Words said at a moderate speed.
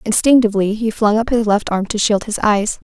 No: fast, 225 wpm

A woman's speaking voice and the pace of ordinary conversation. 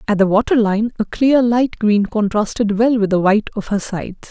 No: female; fast, 210 wpm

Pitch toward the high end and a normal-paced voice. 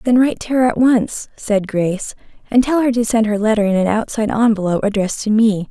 No: high, 220 Hz; fast, 230 wpm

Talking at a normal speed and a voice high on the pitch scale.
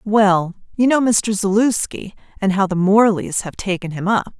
Yes: average, 180 wpm; high, 200 Hz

